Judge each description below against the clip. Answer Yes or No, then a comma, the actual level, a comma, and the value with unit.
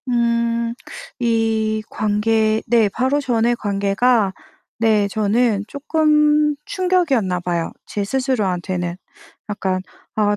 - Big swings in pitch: No, average, 3.5 semitones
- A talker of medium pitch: No, high, 225 Hz